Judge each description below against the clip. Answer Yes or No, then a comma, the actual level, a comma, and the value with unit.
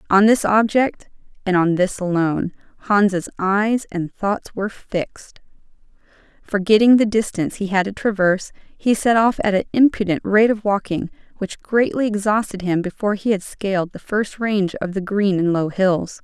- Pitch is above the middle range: Yes, high, 200 Hz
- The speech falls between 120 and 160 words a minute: No, average, 170 wpm